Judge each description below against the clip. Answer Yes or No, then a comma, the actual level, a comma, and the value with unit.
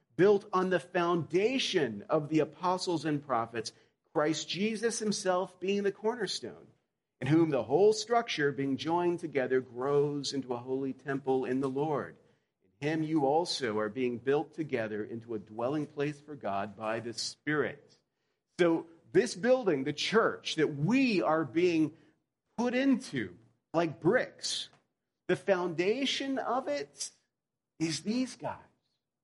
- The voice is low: No, medium, 155 Hz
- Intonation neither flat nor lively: No, wide, 6.0 semitones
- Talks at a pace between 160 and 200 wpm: No, average, 140 wpm